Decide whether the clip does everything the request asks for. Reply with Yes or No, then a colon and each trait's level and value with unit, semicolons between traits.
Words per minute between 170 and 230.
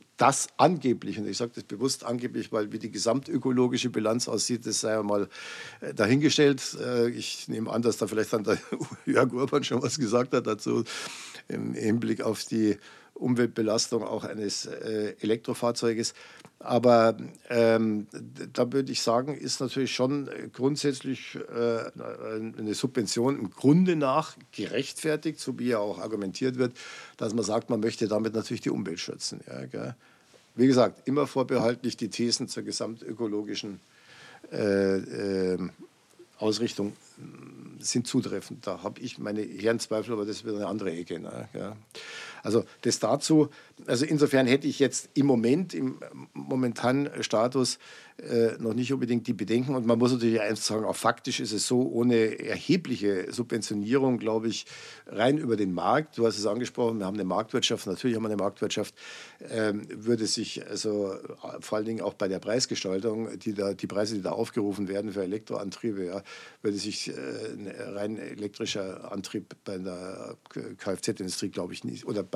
No: average, 160 wpm